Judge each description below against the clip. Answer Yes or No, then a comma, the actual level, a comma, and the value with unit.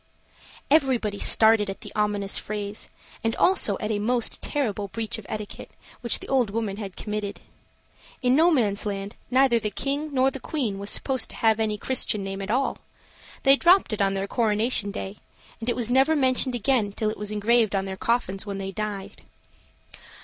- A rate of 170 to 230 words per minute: Yes, average, 180 wpm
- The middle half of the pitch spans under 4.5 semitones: Yes, average, 3.9 semitones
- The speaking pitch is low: No, high, 215 Hz